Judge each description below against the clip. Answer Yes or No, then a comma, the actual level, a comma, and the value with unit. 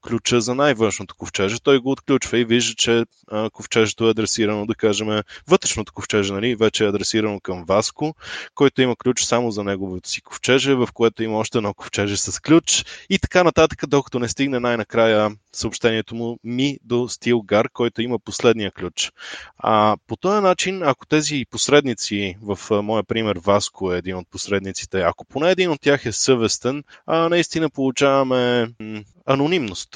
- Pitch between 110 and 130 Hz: Yes, low, 115 Hz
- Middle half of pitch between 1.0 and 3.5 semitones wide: No, average, 4.3 semitones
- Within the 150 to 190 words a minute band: Yes, average, 160 wpm